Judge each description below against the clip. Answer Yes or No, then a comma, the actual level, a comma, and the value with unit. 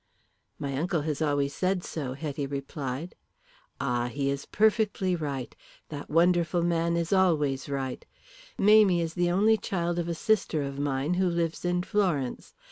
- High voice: No, medium, 165 Hz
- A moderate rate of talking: Yes, average, 155 wpm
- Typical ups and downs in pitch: Yes, average, 4.3 semitones